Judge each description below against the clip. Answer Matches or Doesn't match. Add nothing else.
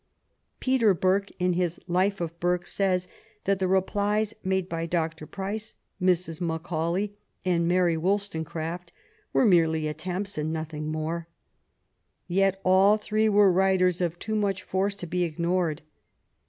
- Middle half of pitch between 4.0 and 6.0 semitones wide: Doesn't match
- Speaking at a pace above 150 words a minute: Doesn't match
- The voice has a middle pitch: Matches